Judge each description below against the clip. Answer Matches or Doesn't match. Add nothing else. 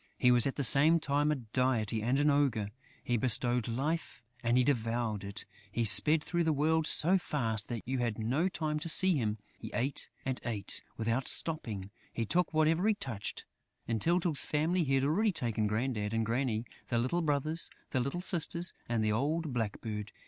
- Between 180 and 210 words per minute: Matches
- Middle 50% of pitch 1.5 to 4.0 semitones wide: Doesn't match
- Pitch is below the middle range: Matches